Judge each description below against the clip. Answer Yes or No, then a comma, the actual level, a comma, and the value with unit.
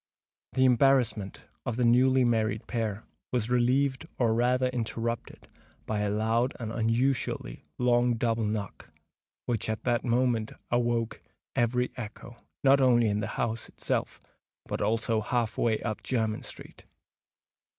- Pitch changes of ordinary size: No, narrow, 2.0 semitones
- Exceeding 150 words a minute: No, slow, 135 wpm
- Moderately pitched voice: No, low, 120 Hz